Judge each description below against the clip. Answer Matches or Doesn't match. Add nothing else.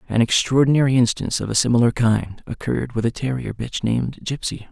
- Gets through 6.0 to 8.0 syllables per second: Matches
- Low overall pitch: Matches